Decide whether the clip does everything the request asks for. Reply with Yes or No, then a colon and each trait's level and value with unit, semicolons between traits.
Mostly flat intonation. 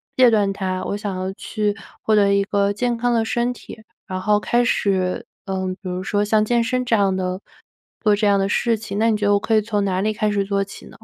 Yes: narrow, 2.2 semitones